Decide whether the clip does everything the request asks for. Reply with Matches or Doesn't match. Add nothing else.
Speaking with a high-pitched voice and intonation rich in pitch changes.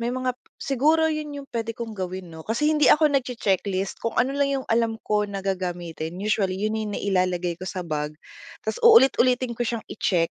Matches